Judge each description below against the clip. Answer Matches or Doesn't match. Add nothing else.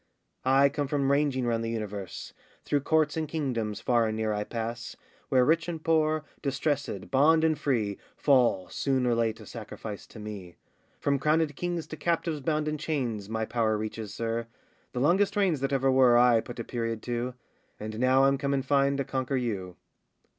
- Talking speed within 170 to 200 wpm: Matches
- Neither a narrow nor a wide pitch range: Matches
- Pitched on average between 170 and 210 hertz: Doesn't match